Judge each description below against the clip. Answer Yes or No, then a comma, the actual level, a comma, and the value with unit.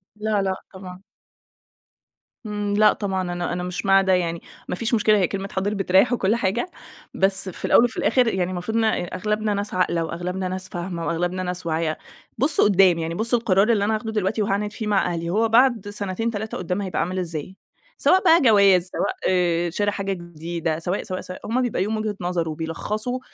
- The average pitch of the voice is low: No, high, 195 Hz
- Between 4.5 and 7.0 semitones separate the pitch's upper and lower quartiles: No, average, 3.1 semitones